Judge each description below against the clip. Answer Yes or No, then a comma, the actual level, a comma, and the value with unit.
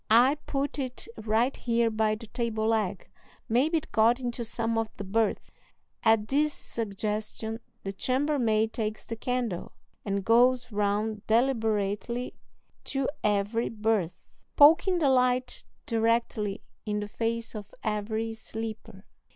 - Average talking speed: No, slow, 130 wpm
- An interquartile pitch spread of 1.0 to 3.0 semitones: Yes, narrow, 2.5 semitones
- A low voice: No, high, 225 Hz